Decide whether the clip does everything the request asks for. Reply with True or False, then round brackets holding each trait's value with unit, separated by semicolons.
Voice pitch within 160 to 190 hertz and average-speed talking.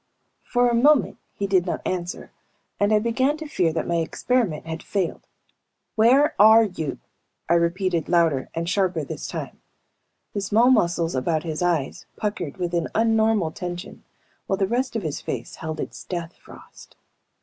True (185 Hz; 165 wpm)